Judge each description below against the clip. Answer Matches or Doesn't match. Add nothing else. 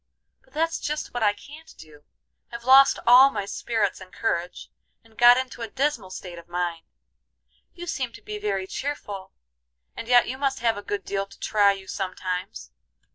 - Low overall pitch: Doesn't match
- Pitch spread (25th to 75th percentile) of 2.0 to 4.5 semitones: Doesn't match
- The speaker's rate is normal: Matches